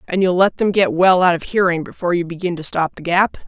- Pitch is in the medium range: Yes, medium, 180 Hz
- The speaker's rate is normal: No, fast, 275 wpm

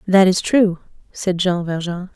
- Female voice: Yes, female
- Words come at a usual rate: Yes, average, 165 wpm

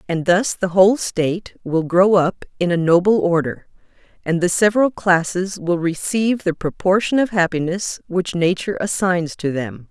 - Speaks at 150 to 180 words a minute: Yes, average, 165 wpm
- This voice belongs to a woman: Yes, female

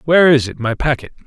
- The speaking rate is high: Yes, fast, 235 wpm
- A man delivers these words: Yes, male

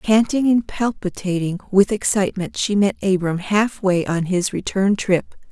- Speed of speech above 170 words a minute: No, average, 140 wpm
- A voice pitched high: Yes, high, 195 Hz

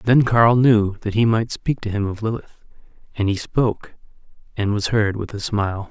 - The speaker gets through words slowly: No, fast, 205 wpm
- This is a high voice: No, low, 110 Hz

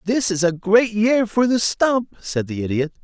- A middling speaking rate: No, fast, 220 wpm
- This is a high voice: Yes, high, 200 Hz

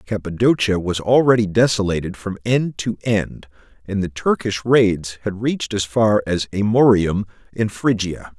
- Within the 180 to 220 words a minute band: No, average, 145 wpm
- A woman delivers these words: No, male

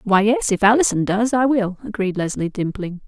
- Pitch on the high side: Yes, high, 210 Hz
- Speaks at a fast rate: No, average, 195 wpm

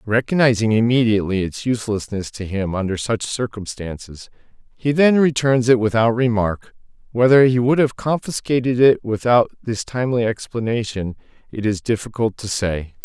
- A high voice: No, low, 115 Hz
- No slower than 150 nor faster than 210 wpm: No, average, 140 wpm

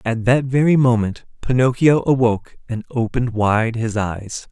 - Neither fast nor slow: Yes, average, 145 wpm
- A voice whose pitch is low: Yes, low, 120 Hz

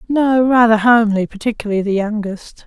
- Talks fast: No, slow, 135 wpm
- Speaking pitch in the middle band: No, high, 220 Hz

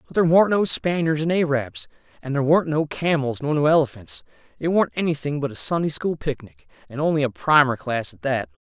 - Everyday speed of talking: No, fast, 215 wpm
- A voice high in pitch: No, medium, 145 Hz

